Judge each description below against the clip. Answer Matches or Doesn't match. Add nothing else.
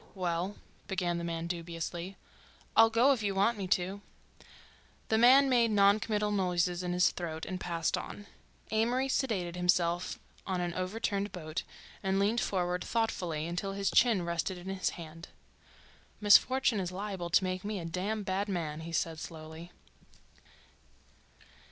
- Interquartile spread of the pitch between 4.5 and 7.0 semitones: Doesn't match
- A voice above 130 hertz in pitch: Matches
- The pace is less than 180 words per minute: Matches